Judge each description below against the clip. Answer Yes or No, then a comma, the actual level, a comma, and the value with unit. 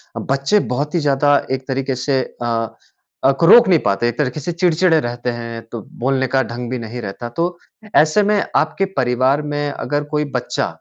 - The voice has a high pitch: No, low, 135 Hz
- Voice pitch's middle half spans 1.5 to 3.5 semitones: No, average, 4.1 semitones